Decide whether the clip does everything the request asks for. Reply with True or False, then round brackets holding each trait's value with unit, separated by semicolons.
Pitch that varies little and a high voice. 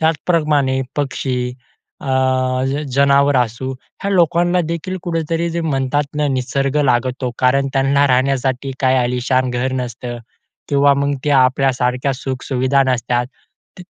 False (2.3 semitones; 135 Hz)